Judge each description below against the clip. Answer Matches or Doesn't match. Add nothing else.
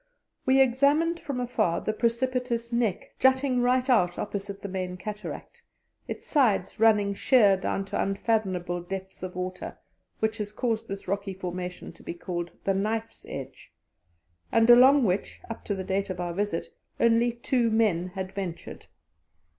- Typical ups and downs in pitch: Matches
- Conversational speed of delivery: Matches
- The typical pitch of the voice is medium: Doesn't match